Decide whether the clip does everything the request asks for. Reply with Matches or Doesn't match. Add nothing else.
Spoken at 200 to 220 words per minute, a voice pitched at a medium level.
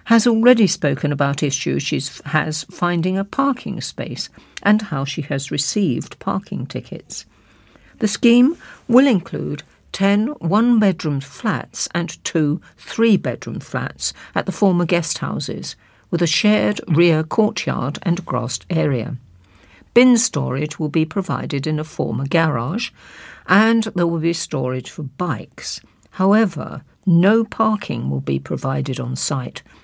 Doesn't match